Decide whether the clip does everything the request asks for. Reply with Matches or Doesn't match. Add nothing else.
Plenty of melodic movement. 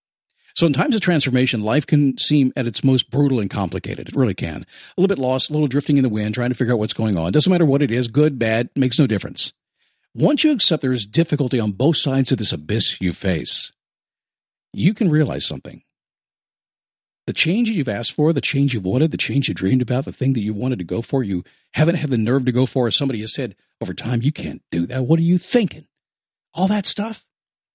Doesn't match